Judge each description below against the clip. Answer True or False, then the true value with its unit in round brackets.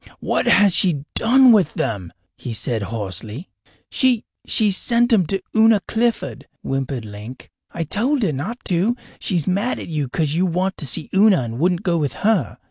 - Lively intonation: True (8.2 semitones)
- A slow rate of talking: False (180 wpm)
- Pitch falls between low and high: True (175 Hz)